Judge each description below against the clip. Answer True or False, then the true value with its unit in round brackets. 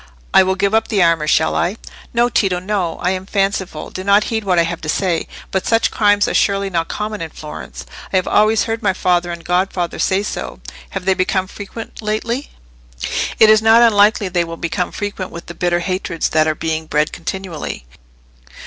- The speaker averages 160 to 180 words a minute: False (195 wpm)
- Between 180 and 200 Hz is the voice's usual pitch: True (190 Hz)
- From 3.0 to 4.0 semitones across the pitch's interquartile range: True (3.4 semitones)